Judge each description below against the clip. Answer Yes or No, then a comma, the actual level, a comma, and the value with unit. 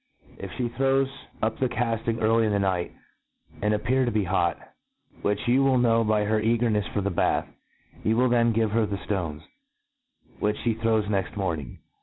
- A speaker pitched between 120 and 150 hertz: No, low, 110 Hz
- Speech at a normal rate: Yes, average, 185 wpm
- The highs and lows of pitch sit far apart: No, narrow, 2.5 semitones